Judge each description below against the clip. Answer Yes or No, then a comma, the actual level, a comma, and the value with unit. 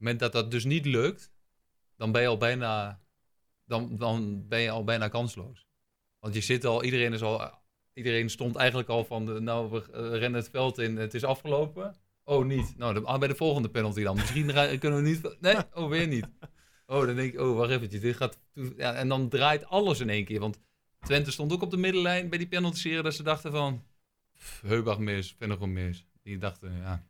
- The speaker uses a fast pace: Yes, fast, 215 wpm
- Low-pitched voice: Yes, low, 120 Hz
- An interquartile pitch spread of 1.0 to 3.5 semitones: No, average, 4.5 semitones